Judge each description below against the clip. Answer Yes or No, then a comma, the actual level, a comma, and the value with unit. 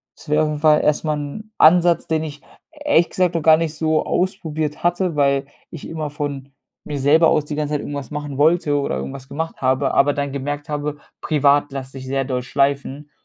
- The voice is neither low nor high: Yes, medium, 150 Hz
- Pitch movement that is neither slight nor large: No, narrow, 2.2 semitones